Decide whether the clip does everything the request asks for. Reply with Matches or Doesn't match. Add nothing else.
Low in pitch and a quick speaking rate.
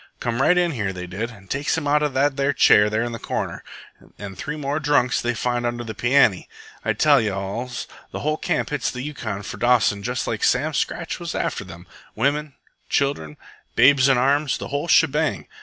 Matches